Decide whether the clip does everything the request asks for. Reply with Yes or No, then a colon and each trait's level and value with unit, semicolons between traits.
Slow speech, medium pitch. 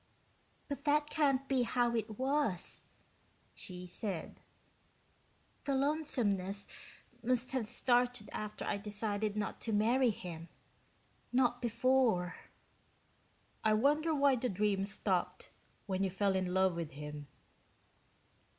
No: slow, 115 wpm; high, 220 Hz